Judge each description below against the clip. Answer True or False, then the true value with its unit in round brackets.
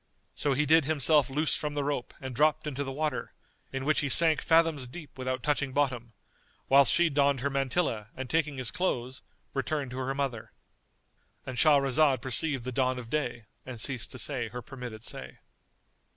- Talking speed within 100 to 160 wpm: False (180 wpm)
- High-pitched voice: False (135 Hz)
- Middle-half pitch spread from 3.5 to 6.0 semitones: False (2.8 semitones)